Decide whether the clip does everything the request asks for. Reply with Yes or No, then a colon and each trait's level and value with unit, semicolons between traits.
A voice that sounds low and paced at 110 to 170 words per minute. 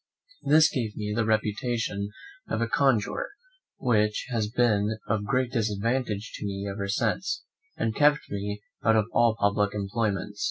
Yes: low, 110 Hz; average, 155 wpm